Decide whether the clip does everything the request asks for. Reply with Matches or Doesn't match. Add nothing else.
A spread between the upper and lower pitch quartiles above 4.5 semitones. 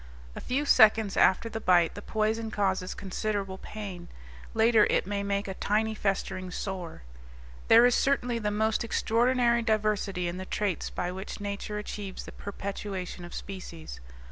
Doesn't match